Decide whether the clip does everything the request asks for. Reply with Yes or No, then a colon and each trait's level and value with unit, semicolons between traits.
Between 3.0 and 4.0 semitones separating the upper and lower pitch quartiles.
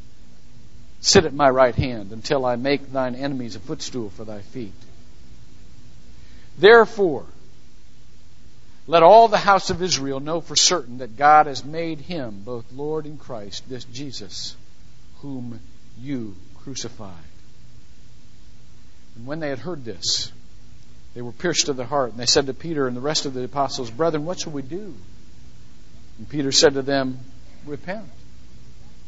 No: average, 4.6 semitones